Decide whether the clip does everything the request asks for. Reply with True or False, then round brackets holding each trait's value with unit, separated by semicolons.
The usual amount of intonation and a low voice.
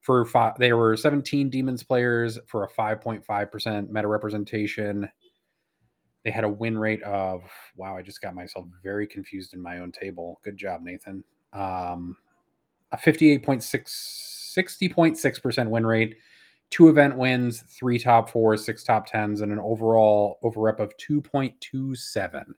True (3.8 semitones; 110 Hz)